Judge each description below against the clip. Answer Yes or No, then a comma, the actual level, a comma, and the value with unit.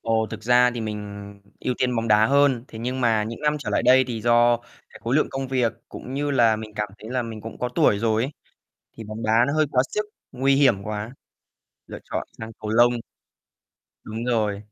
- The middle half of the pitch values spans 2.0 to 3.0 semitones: Yes, average, 2.7 semitones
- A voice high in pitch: No, low, 115 Hz